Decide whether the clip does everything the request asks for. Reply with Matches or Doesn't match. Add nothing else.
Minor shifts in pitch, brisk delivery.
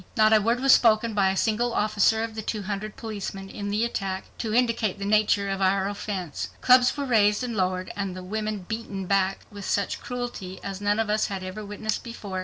Matches